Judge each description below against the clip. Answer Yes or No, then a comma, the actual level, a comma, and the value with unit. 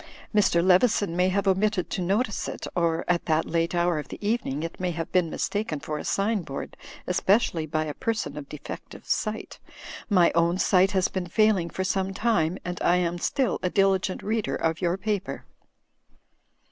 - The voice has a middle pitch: Yes, medium, 180 Hz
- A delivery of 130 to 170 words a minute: No, average, 185 wpm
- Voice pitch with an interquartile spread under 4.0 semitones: Yes, average, 3.2 semitones